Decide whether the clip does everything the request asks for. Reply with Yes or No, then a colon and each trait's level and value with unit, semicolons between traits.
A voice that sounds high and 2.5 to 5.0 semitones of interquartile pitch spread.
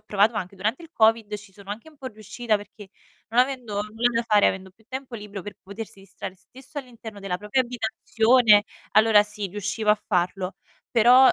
Yes: high, 215 Hz; average, 2.8 semitones